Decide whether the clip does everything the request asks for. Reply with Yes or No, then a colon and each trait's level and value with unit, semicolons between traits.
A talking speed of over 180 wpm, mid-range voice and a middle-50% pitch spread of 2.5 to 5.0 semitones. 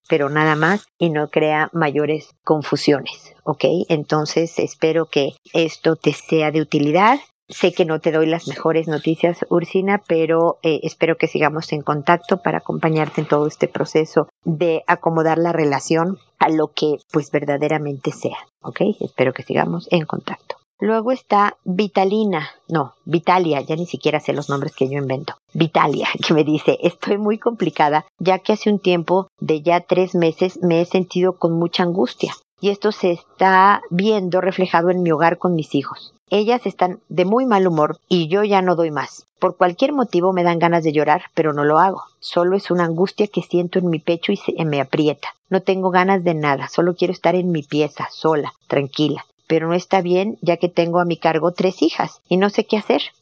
Yes: fast, 190 wpm; medium, 170 Hz; average, 3.3 semitones